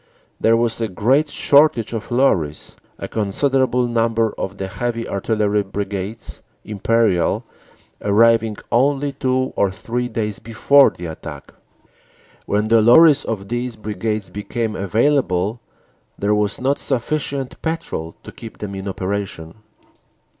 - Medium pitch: No, low, 115 Hz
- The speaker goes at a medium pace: No, slow, 125 wpm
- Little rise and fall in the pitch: No, average, 3.5 semitones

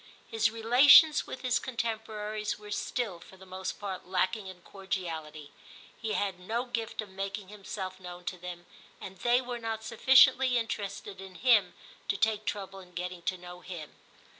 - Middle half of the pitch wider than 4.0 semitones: No, average, 3.6 semitones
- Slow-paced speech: No, average, 165 wpm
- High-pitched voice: Yes, high, 200 Hz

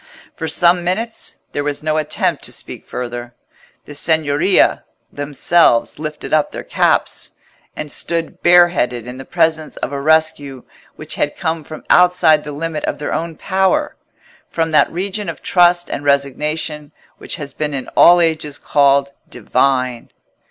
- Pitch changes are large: No, average, 3.2 semitones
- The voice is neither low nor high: Yes, medium, 155 Hz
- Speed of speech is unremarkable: Yes, average, 150 wpm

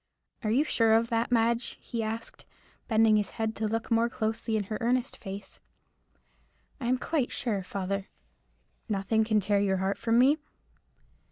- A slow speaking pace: No, average, 165 wpm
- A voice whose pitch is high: Yes, high, 225 Hz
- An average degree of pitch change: No, narrow, 2.2 semitones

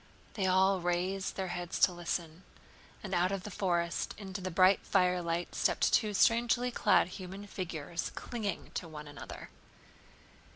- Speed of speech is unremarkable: Yes, average, 150 wpm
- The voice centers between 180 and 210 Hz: Yes, medium, 185 Hz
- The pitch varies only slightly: Yes, narrow, 2.1 semitones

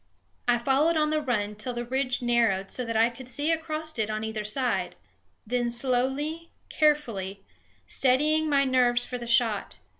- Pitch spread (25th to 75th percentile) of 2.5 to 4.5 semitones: Yes, average, 4.1 semitones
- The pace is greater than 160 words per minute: Yes, average, 170 wpm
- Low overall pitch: No, very high, 250 Hz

